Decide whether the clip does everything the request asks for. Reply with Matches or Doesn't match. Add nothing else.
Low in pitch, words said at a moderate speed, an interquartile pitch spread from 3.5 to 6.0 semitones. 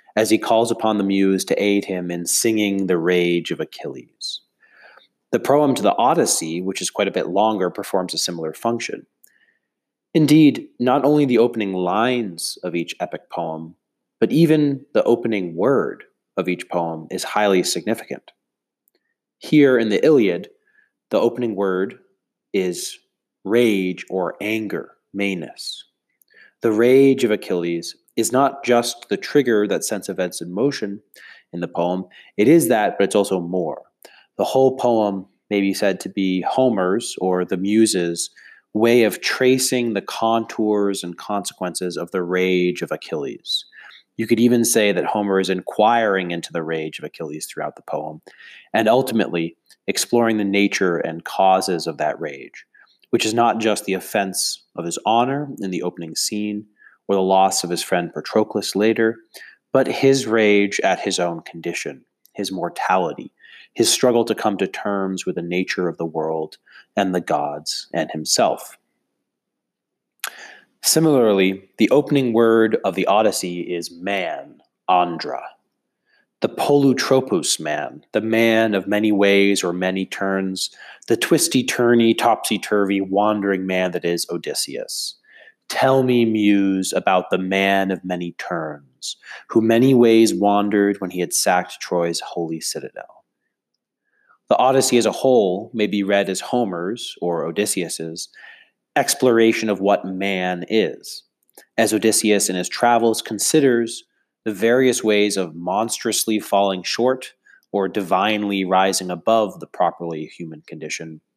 Matches